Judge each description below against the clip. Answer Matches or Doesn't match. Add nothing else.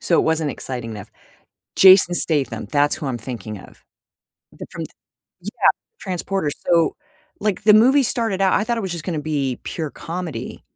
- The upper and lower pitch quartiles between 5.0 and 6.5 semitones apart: Matches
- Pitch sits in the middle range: Matches